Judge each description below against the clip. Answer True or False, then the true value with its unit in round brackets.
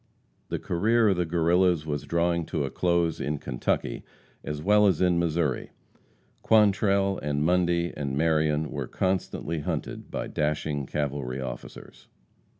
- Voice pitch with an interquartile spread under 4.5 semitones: True (3.5 semitones)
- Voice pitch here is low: True (85 Hz)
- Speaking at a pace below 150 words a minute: True (140 wpm)